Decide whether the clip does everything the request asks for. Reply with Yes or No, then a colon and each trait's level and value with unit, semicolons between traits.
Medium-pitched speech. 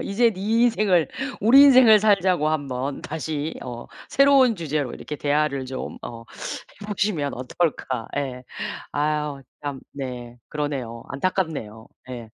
Yes: medium, 150 Hz